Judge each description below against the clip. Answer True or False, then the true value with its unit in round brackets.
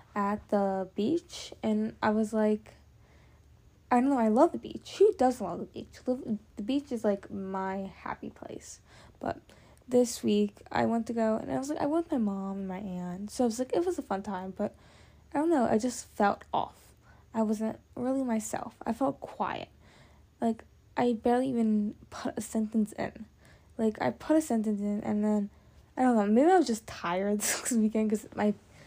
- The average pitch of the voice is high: True (220 Hz)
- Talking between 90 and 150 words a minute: False (200 wpm)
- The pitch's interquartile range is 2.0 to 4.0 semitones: True (3.4 semitones)